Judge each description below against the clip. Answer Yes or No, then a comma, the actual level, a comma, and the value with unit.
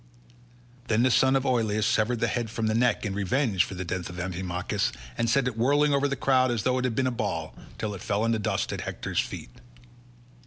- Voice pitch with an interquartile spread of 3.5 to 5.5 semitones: Yes, average, 4.1 semitones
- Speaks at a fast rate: Yes, fast, 235 wpm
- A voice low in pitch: Yes, low, 115 Hz